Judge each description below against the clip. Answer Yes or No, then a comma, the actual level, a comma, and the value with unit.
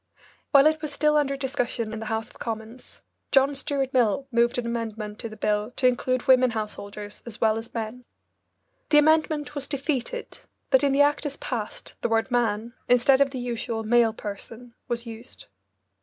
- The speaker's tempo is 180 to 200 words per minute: Yes, average, 185 wpm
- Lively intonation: No, average, 3.6 semitones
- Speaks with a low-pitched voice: No, high, 240 Hz